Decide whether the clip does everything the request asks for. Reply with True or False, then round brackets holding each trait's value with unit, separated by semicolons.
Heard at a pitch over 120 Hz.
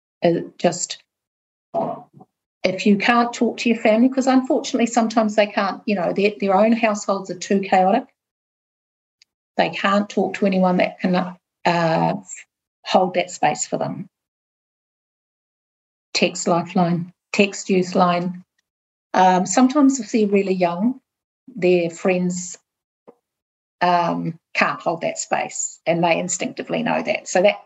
True (190 Hz)